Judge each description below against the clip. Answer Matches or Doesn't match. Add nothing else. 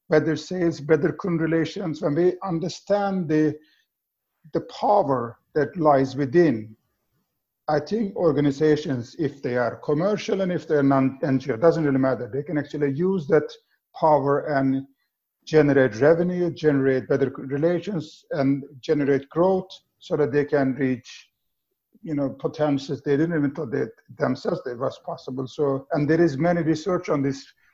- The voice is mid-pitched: Matches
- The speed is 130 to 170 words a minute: Matches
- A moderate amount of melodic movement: Matches